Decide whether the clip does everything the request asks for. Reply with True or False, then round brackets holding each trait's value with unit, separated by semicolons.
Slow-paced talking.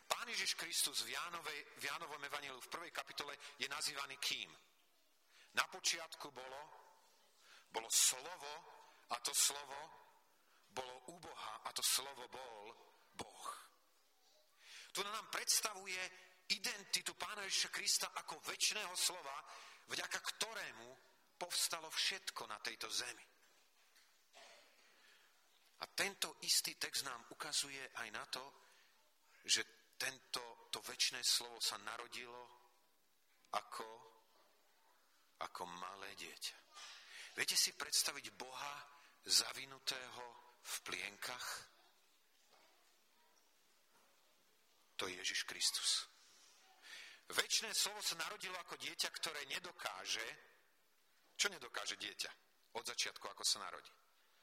True (100 wpm)